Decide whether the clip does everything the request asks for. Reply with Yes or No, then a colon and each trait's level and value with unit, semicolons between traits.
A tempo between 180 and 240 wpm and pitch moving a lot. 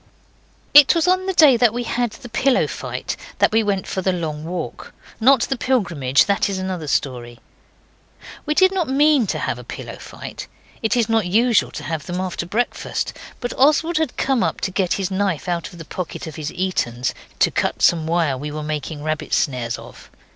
Yes: average, 200 wpm; wide, 7.6 semitones